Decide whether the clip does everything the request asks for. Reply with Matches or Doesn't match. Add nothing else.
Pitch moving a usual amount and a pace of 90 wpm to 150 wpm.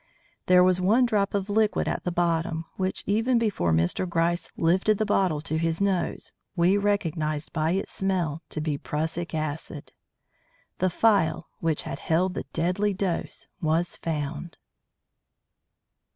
Matches